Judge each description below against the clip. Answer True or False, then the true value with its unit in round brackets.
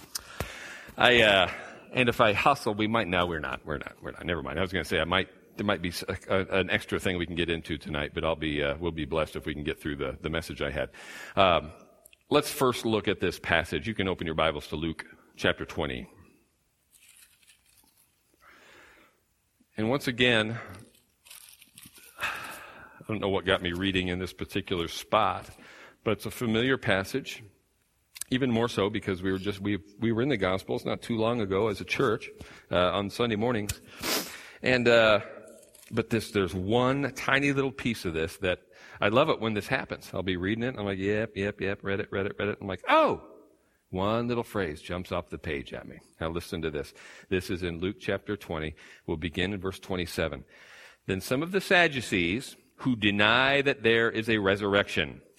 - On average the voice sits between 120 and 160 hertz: False (100 Hz)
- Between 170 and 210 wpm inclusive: True (200 wpm)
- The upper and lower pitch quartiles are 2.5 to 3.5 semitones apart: False (4.2 semitones)